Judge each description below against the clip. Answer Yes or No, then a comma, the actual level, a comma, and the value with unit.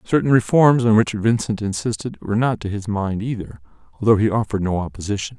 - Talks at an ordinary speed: Yes, average, 190 wpm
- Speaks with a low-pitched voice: Yes, low, 105 Hz